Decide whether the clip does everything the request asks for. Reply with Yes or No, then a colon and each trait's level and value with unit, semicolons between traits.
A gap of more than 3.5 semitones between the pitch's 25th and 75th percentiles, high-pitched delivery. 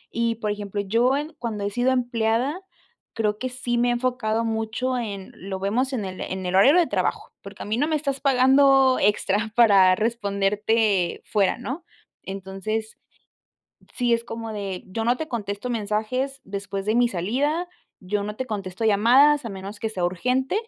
Yes: average, 3.9 semitones; high, 225 Hz